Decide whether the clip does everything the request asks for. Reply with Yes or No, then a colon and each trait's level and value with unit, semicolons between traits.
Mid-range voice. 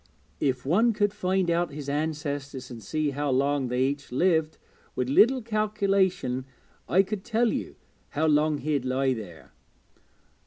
Yes: medium, 150 Hz